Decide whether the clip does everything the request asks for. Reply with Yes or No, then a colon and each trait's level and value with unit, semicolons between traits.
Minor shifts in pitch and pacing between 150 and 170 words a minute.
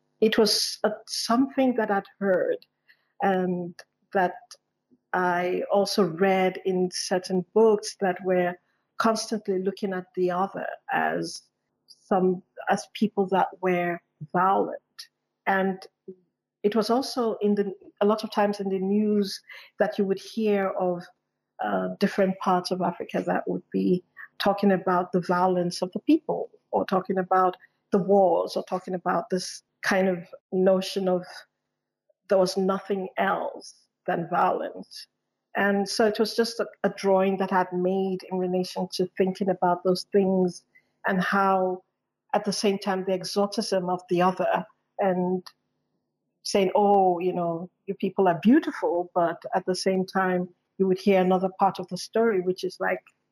Yes: narrow, 1.9 semitones; average, 155 wpm